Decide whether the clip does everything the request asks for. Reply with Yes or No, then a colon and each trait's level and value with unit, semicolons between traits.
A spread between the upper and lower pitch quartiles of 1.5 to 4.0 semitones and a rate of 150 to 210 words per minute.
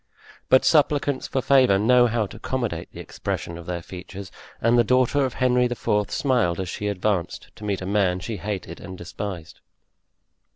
No: average, 5.2 semitones; average, 175 wpm